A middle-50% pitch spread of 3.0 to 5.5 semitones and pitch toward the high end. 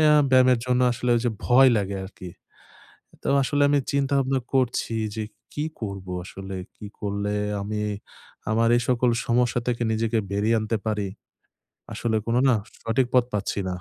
No: average, 3.3 semitones; low, 115 Hz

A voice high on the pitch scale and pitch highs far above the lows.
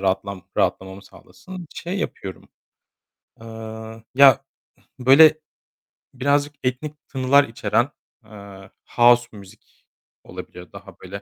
No: low, 120 Hz; wide, 5.8 semitones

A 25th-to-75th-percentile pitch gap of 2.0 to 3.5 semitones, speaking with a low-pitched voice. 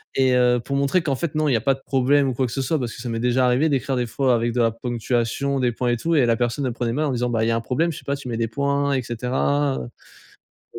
Yes: narrow, 2.6 semitones; low, 125 Hz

